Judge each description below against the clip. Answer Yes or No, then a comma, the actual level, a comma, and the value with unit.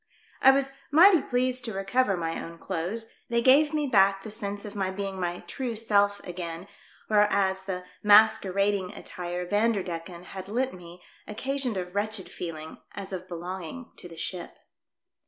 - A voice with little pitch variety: No, average, 4.0 semitones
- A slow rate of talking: No, average, 160 wpm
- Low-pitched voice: No, high, 200 Hz